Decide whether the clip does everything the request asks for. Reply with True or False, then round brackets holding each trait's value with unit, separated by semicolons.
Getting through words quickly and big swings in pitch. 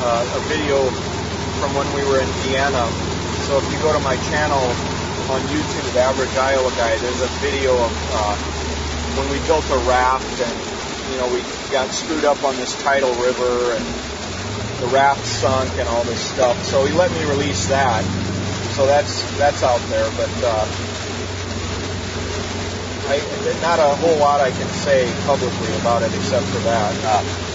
False (170 wpm; 6.0 semitones)